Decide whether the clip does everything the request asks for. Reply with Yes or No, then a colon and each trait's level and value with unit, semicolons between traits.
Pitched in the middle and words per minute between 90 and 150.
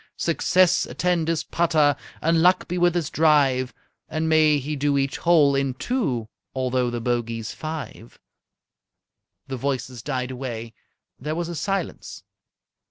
Yes: medium, 145 Hz; average, 140 wpm